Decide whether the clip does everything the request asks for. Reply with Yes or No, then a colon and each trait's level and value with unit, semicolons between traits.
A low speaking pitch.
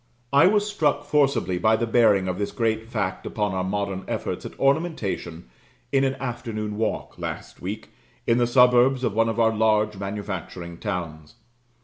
Yes: low, 110 Hz